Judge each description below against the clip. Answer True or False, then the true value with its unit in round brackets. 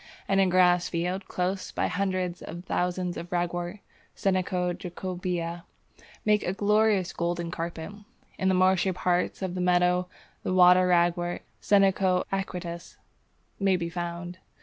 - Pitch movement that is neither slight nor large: False (1.3 semitones)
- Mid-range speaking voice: True (180 Hz)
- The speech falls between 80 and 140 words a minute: True (135 wpm)